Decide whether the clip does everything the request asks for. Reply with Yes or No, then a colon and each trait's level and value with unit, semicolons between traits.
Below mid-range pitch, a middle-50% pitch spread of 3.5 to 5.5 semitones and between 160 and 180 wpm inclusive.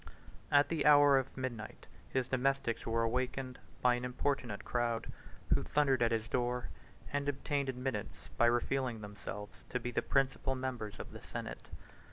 No: low, 125 Hz; narrow, 2.5 semitones; average, 165 wpm